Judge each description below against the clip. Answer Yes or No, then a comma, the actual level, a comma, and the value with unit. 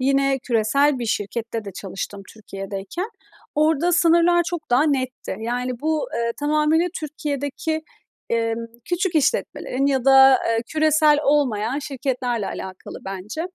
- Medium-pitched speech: No, very high, 270 Hz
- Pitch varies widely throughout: No, average, 5.0 semitones